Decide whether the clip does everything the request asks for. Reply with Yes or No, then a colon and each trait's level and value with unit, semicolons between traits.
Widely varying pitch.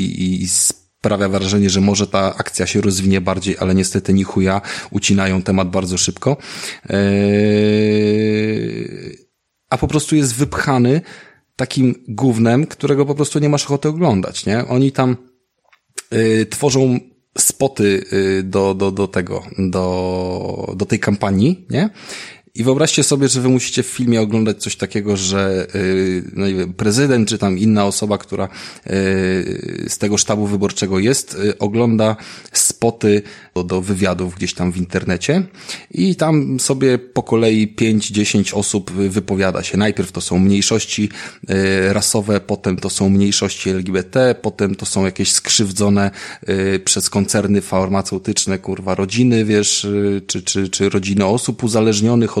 No: average, 3.6 semitones